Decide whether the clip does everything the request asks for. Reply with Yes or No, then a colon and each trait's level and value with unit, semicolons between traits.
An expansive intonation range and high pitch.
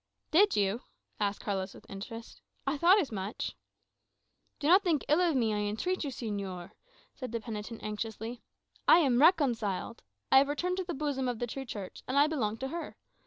Yes: wide, 6.3 semitones; high, 245 Hz